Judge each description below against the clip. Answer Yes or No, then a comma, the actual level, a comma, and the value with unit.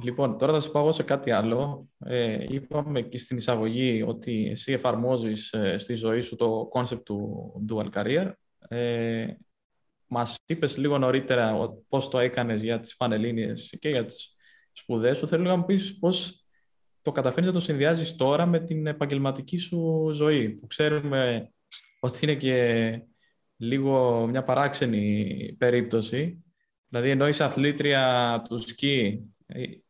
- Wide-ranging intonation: No, average, 4.2 semitones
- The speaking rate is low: No, average, 145 wpm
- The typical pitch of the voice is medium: No, low, 125 Hz